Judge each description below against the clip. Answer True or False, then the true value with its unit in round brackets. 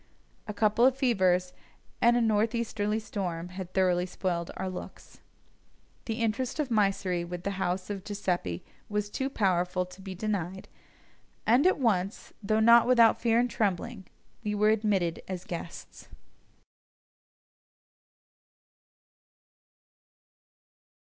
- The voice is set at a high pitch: True (200 Hz)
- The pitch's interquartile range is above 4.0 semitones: False (3.7 semitones)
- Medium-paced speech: False (120 wpm)